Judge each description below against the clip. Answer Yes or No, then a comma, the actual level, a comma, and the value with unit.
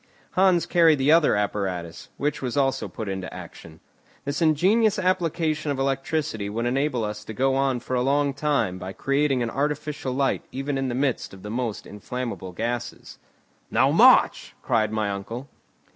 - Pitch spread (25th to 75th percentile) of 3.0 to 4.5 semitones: No, average, 5.2 semitones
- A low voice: Yes, low, 130 Hz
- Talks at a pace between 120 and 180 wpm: Yes, average, 170 wpm